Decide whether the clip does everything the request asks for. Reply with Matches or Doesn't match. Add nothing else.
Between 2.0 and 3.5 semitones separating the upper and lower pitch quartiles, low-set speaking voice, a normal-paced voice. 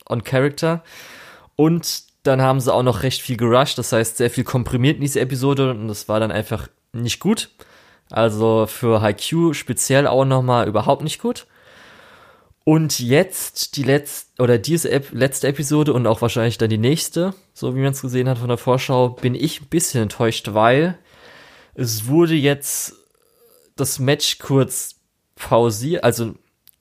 Doesn't match